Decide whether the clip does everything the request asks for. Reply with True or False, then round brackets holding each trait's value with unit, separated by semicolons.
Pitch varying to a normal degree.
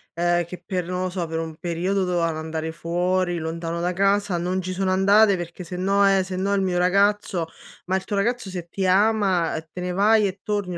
False (2.3 semitones)